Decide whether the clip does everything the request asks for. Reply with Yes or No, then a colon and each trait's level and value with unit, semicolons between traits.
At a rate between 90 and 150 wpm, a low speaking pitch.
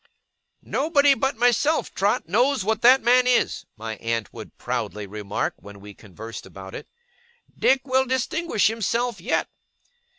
No: average, 140 wpm; high, 225 Hz